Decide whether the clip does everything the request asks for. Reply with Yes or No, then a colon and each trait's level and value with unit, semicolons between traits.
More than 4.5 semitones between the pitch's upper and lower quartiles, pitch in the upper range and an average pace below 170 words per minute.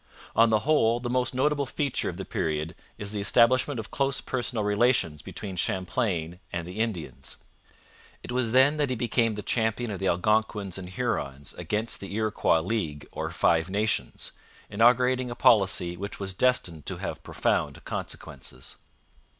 No: average, 5.2 semitones; low, 110 Hz; average, 160 wpm